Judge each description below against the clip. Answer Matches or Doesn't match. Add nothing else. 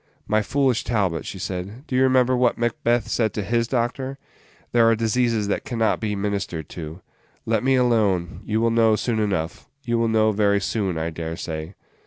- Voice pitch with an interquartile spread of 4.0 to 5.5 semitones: Doesn't match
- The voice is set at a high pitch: Doesn't match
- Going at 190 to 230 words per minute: Matches